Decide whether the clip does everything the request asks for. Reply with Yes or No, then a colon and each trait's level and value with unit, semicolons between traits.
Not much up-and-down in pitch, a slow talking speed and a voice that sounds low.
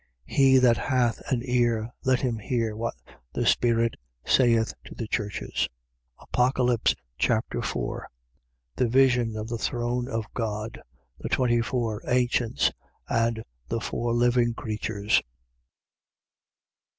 Yes: narrow, 1.7 semitones; slow, 125 wpm; low, 120 Hz